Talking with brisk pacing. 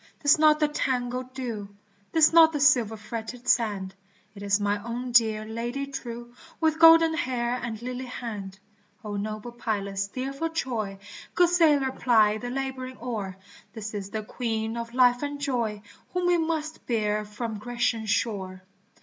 No: average, 160 wpm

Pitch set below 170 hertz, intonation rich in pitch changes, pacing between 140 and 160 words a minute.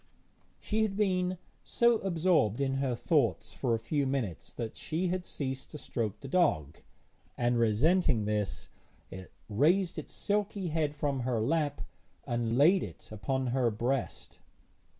Yes: low, 135 Hz; wide, 7.1 semitones; average, 150 wpm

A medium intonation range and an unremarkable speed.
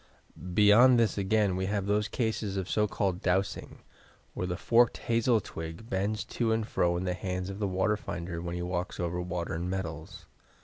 Yes: average, 3.1 semitones; average, 190 wpm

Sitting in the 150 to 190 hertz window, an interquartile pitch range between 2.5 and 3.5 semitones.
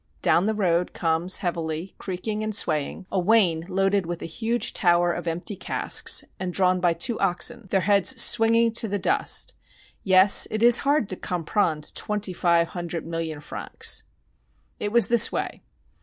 No: medium, 185 Hz; average, 3.9 semitones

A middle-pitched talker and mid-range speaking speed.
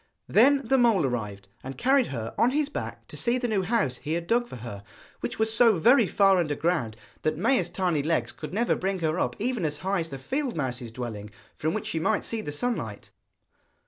No: medium, 180 Hz; fast, 220 wpm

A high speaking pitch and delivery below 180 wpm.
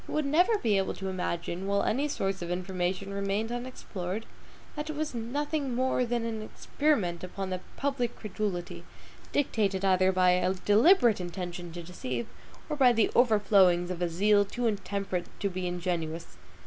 Yes: high, 200 Hz; average, 165 wpm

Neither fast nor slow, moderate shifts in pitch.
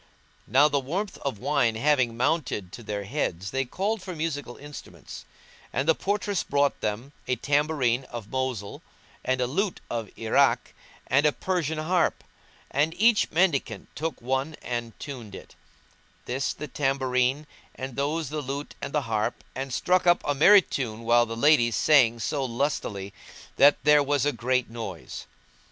Yes: average, 160 wpm; average, 4.3 semitones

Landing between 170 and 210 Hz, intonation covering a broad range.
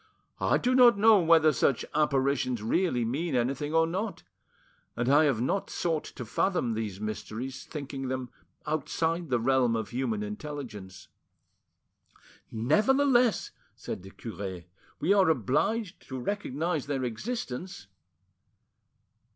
No: medium, 140 Hz; wide, 6.5 semitones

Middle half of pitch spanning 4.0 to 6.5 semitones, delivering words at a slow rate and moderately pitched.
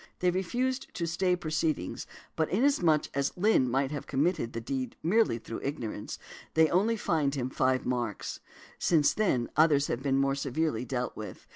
No: average, 5.3 semitones; average, 165 wpm; medium, 145 Hz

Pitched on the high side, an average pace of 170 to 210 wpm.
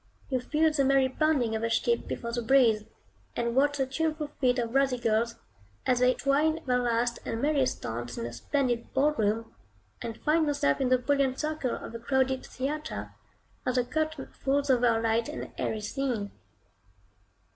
Yes: very high, 255 Hz; average, 180 wpm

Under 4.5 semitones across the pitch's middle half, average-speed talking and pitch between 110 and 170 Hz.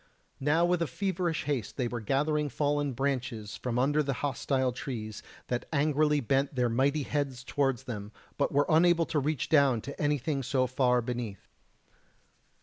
Yes: average, 3.1 semitones; average, 155 wpm; medium, 140 Hz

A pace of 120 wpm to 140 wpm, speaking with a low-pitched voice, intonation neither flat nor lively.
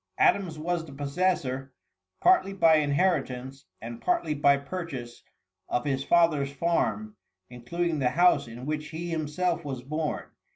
No: slow, 135 wpm; medium, 150 Hz; average, 4.2 semitones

